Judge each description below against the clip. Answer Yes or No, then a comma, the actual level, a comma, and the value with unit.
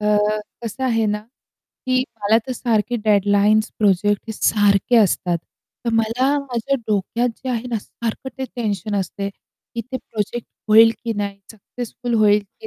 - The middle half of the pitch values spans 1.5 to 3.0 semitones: Yes, average, 2.7 semitones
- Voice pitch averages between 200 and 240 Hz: Yes, high, 220 Hz